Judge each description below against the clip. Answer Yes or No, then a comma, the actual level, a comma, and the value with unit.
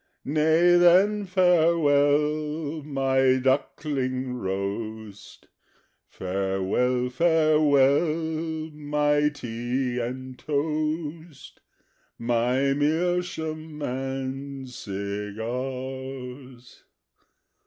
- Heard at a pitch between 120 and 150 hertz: Yes, medium, 140 Hz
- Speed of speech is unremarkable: No, slow, 55 wpm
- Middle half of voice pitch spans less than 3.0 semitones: No, average, 3.7 semitones